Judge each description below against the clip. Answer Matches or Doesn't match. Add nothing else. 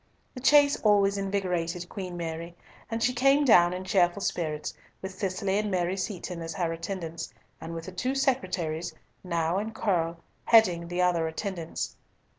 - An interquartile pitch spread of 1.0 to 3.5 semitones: Matches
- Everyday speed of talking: Matches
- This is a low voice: Doesn't match